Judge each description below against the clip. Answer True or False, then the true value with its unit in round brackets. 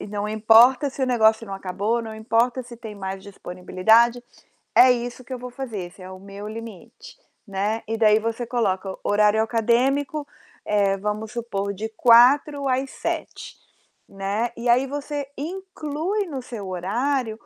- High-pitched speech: True (230 Hz)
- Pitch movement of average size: True (3.8 semitones)